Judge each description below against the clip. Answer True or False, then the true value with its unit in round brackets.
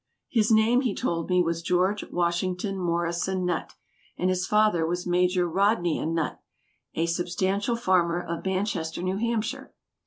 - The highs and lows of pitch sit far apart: False (2.8 semitones)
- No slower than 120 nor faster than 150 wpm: True (145 wpm)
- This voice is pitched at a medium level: True (180 Hz)